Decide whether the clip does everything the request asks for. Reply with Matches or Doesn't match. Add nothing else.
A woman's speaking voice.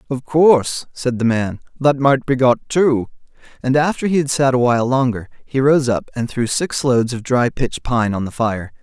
Doesn't match